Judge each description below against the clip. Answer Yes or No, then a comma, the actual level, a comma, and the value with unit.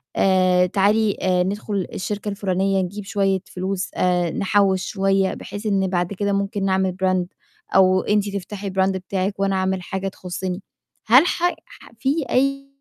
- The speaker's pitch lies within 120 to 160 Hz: No, high, 195 Hz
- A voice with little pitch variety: Yes, narrow, 1.5 semitones